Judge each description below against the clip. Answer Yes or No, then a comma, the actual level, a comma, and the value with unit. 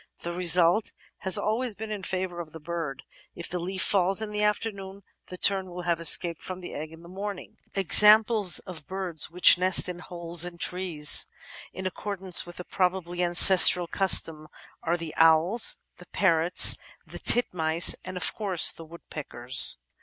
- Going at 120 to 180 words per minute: Yes, average, 170 wpm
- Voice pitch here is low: No, medium, 180 Hz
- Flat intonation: Yes, narrow, 2.3 semitones